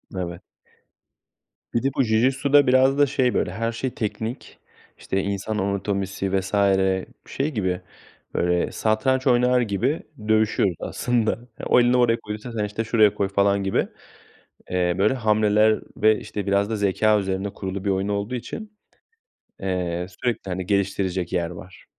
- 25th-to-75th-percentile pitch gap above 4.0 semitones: No, average, 3.7 semitones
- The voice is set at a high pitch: No, low, 105 Hz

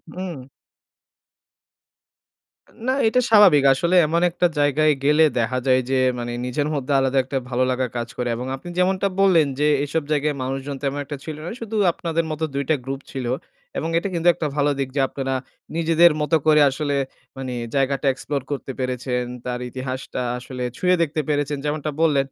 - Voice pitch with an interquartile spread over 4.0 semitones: No, average, 3.5 semitones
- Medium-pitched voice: Yes, medium, 145 Hz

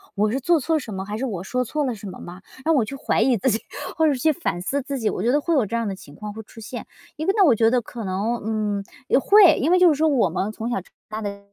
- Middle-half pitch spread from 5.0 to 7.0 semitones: Yes, wide, 5.5 semitones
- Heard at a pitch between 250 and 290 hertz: No, high, 235 Hz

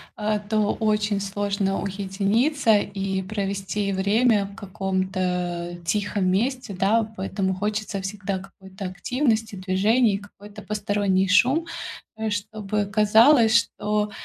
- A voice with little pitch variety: Yes, narrow, 1.9 semitones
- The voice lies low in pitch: No, high, 205 Hz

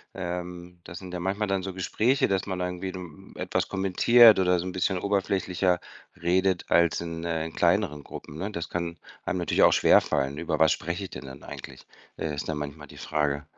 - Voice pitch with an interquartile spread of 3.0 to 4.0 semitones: No, narrow, 2.5 semitones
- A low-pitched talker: Yes, very low, 90 Hz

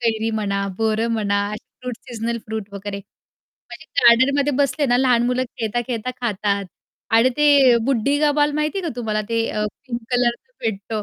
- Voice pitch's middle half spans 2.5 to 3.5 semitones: Yes, average, 2.9 semitones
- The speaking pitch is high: Yes, high, 235 Hz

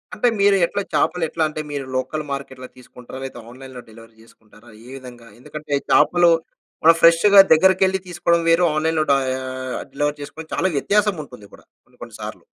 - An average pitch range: Yes, average, 4.8 semitones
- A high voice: No, medium, 150 Hz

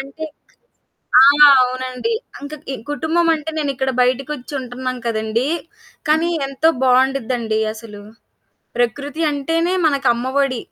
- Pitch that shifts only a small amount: No, average, 3.1 semitones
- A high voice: Yes, very high, 265 Hz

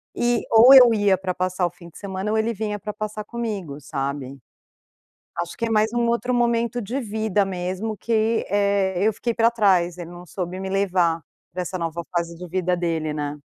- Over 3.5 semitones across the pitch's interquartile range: Yes, average, 4.0 semitones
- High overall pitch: Yes, high, 195 Hz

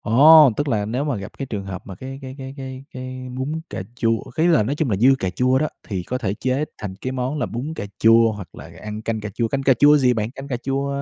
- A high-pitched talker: No, low, 130 Hz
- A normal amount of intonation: Yes, average, 3.8 semitones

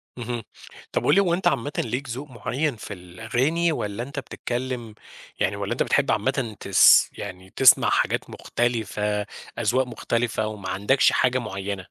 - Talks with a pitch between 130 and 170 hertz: No, low, 120 Hz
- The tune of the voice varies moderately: Yes, average, 3.9 semitones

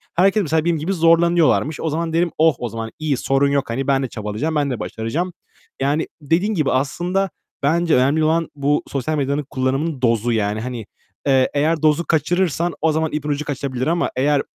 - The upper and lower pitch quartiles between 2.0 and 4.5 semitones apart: Yes, average, 3.7 semitones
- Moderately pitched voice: Yes, medium, 150 Hz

